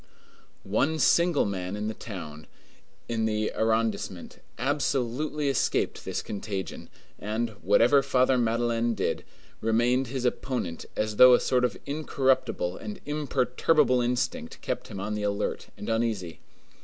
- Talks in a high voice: No, low, 120 Hz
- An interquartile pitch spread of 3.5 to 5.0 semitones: Yes, average, 4.0 semitones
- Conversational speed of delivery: No, slow, 130 wpm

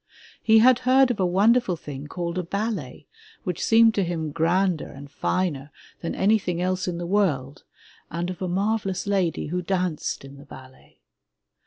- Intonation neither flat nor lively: Yes, average, 3.9 semitones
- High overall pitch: No, medium, 180 Hz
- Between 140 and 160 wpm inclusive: No, average, 175 wpm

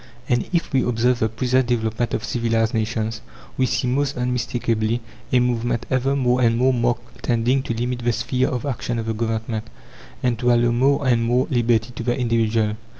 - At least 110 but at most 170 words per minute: No, average, 190 wpm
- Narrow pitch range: Yes, narrow, 1.7 semitones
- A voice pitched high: No, low, 120 Hz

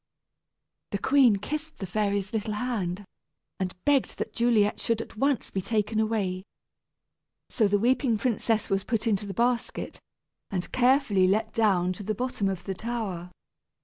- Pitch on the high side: Yes, high, 215 Hz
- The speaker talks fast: No, average, 155 wpm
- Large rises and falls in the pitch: No, average, 3.4 semitones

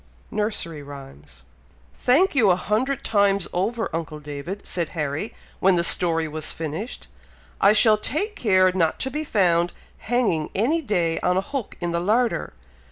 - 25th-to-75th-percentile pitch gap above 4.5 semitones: Yes, wide, 5.5 semitones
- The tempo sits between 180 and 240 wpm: No, average, 160 wpm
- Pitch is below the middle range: No, medium, 185 Hz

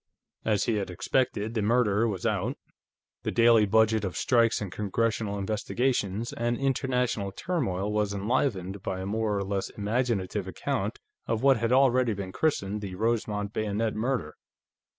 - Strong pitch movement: No, average, 2.9 semitones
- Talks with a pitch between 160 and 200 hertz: No, low, 110 Hz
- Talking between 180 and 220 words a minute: No, average, 150 wpm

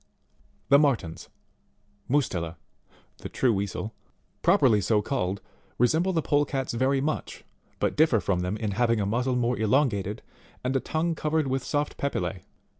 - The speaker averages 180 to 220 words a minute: No, average, 145 wpm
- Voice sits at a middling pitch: No, low, 125 Hz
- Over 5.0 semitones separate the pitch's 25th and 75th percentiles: Yes, wide, 5.6 semitones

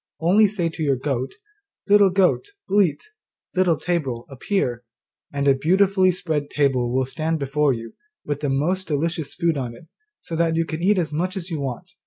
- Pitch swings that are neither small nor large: Yes, average, 4.8 semitones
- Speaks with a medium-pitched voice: Yes, medium, 160 Hz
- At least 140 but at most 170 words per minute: No, average, 185 wpm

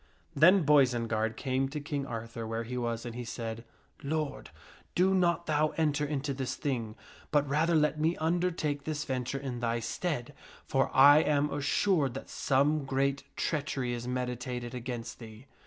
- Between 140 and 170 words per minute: Yes, average, 165 wpm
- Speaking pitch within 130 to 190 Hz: Yes, low, 135 Hz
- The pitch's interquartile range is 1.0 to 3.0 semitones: No, average, 3.8 semitones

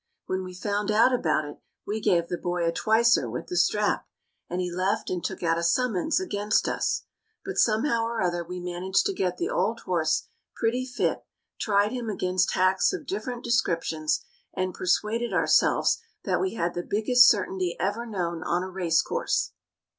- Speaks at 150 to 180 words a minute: Yes, average, 175 wpm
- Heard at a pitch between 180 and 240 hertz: Yes, high, 190 Hz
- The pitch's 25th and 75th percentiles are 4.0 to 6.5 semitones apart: Yes, average, 4.6 semitones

